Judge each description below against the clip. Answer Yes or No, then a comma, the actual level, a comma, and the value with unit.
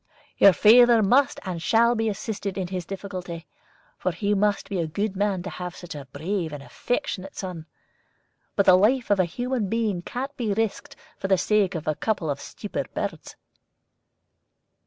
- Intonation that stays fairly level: No, average, 3.6 semitones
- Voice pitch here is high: Yes, high, 195 Hz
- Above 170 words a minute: Yes, average, 180 wpm